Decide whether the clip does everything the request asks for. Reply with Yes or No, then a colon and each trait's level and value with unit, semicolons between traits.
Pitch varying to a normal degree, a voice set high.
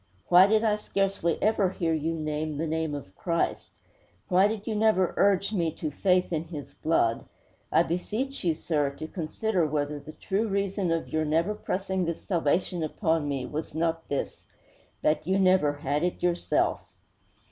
No: average, 3.8 semitones; medium, 170 Hz